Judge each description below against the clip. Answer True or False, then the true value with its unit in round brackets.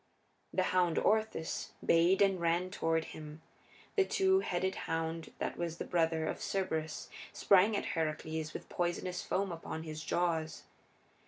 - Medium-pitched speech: True (170 Hz)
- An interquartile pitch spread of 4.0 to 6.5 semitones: False (2.6 semitones)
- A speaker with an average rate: True (145 wpm)